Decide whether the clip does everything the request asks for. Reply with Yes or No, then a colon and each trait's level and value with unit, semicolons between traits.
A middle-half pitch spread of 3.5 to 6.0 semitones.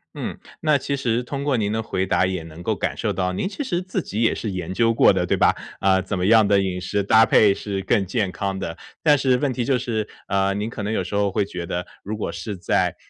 Yes: average, 3.8 semitones